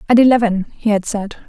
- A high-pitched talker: Yes, high, 215 Hz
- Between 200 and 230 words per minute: Yes, fast, 205 wpm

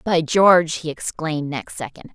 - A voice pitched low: No, medium, 160 Hz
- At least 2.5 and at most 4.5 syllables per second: No, 5.0 syllables/s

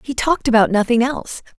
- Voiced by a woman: Yes, female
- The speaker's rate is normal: Yes, average, 190 wpm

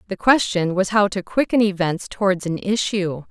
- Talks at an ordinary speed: Yes, average, 180 wpm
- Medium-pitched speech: No, high, 195 Hz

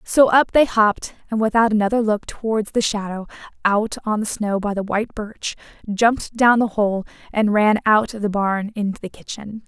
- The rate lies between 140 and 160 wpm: No, average, 200 wpm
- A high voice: Yes, high, 215 Hz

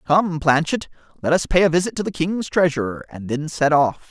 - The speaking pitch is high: No, medium, 160 Hz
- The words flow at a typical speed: No, fast, 220 wpm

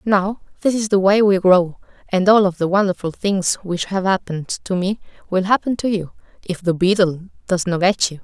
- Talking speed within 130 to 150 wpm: No, fast, 205 wpm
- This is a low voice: No, high, 190 Hz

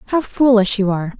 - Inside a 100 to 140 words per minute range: No, average, 200 wpm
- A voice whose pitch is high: Yes, high, 220 Hz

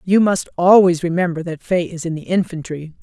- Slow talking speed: No, average, 200 wpm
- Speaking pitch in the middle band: Yes, medium, 175 Hz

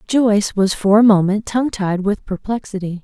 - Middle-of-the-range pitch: No, high, 205 Hz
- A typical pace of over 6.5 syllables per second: No, 5.2 syllables/s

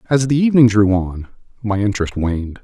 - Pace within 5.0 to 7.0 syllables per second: Yes, 5.9 syllables/s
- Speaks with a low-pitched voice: Yes, low, 110 Hz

